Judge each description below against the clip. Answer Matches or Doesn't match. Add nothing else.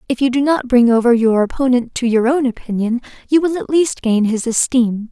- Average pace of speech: Doesn't match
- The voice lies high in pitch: Matches